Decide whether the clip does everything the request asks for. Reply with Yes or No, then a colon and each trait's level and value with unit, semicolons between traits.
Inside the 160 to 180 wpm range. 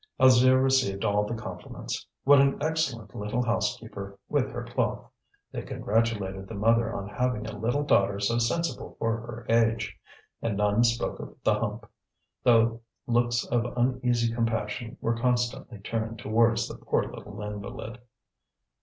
No: average, 145 wpm